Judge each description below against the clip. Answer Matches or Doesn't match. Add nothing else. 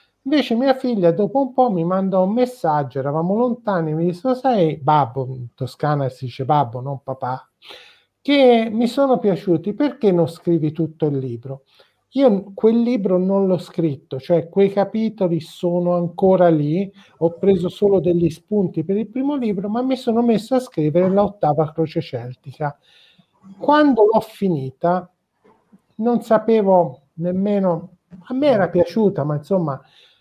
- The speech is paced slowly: Doesn't match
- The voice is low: Doesn't match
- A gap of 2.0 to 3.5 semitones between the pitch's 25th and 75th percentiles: Doesn't match